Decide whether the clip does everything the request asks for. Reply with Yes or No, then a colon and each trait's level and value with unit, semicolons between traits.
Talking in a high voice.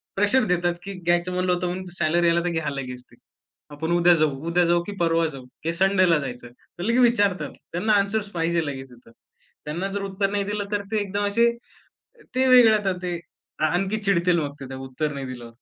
No: medium, 175 Hz